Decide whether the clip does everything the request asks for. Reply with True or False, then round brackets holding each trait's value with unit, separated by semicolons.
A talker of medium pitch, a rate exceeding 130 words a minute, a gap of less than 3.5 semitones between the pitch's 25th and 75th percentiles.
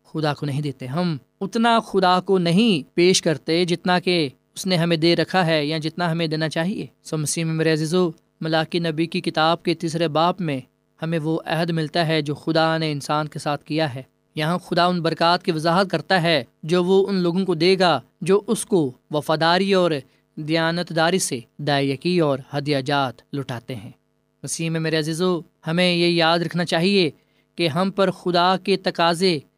True (165 Hz; 185 wpm; 2.6 semitones)